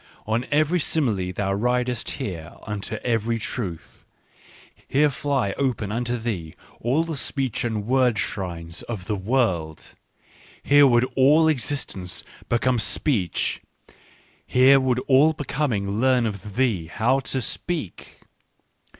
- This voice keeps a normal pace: No, slow, 125 wpm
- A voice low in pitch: Yes, low, 120 Hz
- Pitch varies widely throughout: No, average, 5.0 semitones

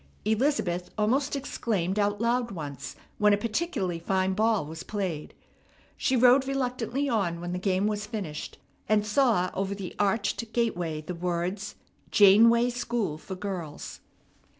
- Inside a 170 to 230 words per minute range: No, average, 140 wpm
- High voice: Yes, high, 205 Hz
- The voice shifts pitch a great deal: No, average, 4.5 semitones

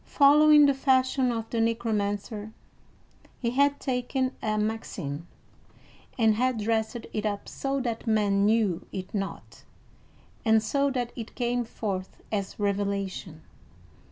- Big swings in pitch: No, average, 3.8 semitones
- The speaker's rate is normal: No, slow, 125 wpm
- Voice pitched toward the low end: No, high, 225 Hz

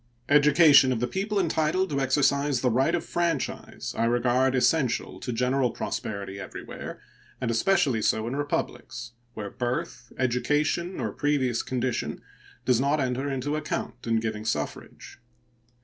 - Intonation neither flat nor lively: Yes, average, 3.8 semitones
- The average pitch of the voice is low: Yes, low, 130 Hz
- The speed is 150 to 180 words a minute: No, average, 140 wpm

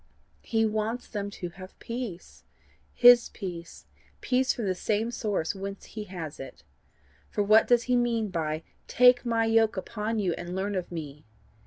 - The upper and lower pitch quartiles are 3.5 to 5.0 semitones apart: Yes, average, 4.1 semitones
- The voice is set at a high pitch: Yes, high, 210 Hz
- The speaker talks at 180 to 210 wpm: No, average, 165 wpm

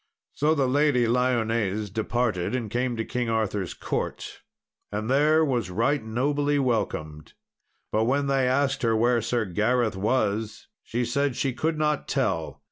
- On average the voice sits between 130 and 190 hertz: No, low, 120 Hz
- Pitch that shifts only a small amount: No, average, 3.8 semitones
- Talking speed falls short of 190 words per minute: Yes, average, 150 wpm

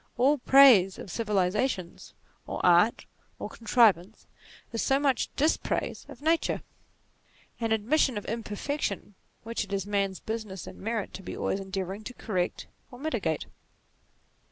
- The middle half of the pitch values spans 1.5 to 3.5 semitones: No, average, 4.4 semitones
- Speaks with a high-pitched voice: Yes, high, 220 Hz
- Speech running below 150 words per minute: Yes, slow, 135 wpm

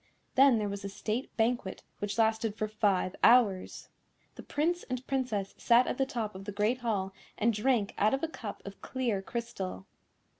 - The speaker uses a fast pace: No, average, 185 wpm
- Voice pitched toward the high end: Yes, high, 220 Hz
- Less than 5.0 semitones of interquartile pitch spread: Yes, average, 3.8 semitones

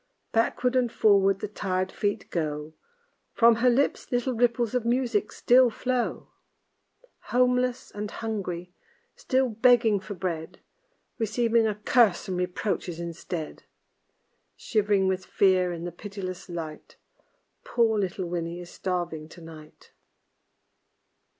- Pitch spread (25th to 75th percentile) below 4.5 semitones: No, average, 4.8 semitones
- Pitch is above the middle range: Yes, high, 205 Hz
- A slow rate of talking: Yes, slow, 120 wpm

